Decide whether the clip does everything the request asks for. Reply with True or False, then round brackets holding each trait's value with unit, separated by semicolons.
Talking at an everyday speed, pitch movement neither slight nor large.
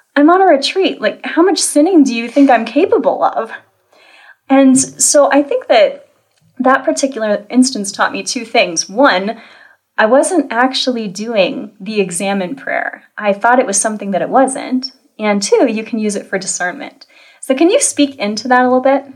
True (185 wpm; 4.7 semitones)